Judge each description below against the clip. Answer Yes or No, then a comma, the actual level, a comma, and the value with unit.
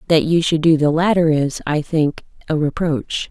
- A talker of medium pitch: Yes, medium, 160 Hz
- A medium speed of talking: Yes, average, 180 wpm